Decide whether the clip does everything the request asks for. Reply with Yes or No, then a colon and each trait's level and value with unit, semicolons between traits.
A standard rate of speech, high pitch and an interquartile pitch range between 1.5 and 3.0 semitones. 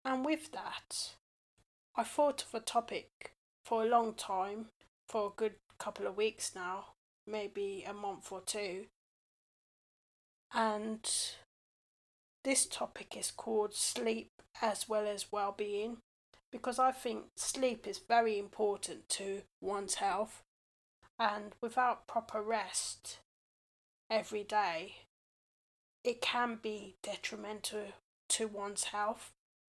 No: slow, 115 wpm; high, 215 Hz; narrow, 2.5 semitones